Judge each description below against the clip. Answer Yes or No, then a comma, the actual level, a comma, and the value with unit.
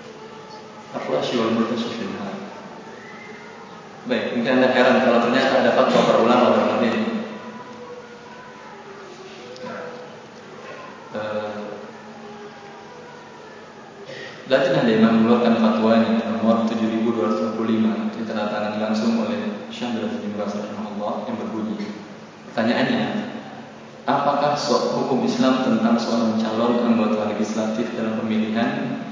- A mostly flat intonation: Yes, narrow, 2.2 semitones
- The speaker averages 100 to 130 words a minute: No, average, 90 wpm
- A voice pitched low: Yes, low, 115 Hz